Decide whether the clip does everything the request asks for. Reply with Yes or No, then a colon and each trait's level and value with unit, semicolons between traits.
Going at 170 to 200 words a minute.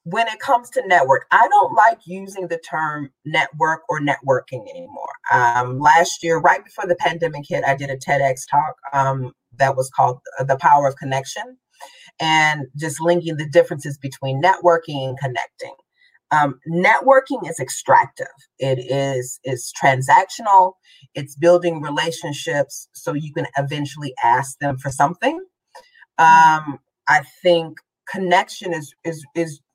No: average, 145 wpm